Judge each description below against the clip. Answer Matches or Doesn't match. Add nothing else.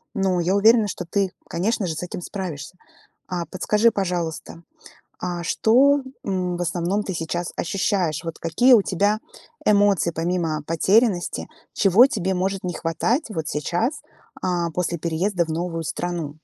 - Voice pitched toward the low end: Doesn't match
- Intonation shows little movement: Doesn't match